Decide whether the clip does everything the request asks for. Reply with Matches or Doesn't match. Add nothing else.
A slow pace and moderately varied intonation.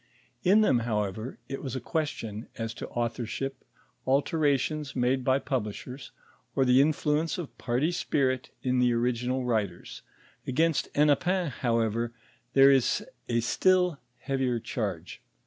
Matches